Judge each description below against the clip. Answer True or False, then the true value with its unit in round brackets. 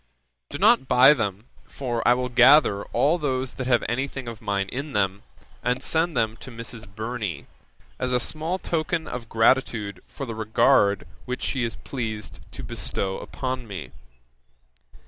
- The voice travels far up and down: False (3.5 semitones)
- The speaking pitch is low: True (120 Hz)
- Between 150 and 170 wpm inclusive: True (160 wpm)